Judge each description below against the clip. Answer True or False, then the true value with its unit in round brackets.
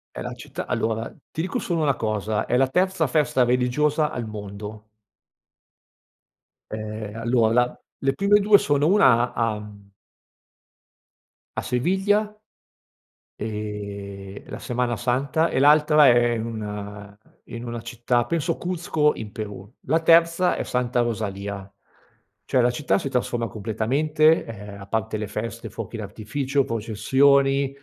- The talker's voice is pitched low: True (120 Hz)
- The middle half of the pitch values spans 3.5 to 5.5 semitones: True (5.1 semitones)